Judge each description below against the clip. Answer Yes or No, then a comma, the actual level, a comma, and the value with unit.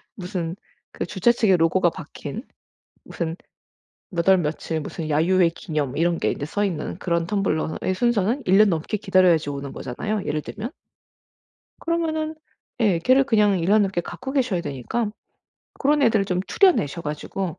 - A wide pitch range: No, average, 4.7 semitones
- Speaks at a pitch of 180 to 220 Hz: Yes, medium, 185 Hz